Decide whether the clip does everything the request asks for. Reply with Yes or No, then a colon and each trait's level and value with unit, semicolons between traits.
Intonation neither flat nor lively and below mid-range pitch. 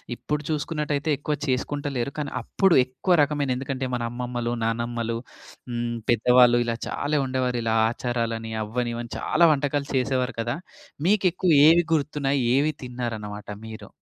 Yes: average, 3.6 semitones; low, 125 Hz